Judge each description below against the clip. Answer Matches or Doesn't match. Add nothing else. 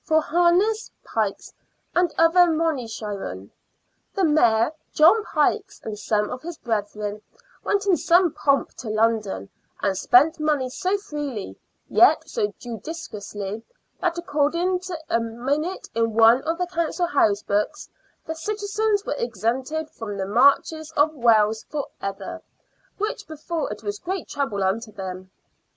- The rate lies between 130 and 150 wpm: Matches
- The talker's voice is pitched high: Matches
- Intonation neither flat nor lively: Doesn't match